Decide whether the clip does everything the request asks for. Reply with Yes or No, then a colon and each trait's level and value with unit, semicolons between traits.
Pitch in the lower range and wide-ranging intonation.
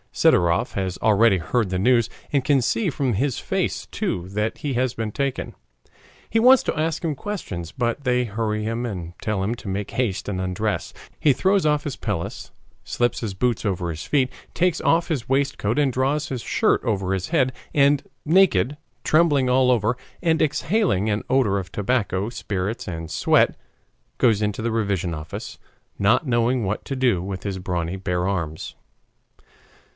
Yes: low, 115 Hz; wide, 6.1 semitones